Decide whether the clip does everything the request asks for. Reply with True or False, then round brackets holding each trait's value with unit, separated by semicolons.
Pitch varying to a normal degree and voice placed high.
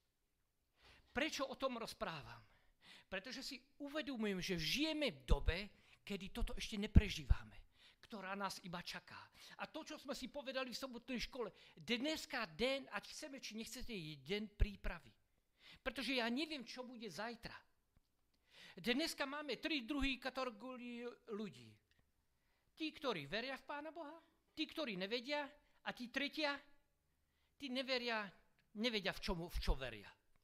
False (5.9 semitones; 240 Hz)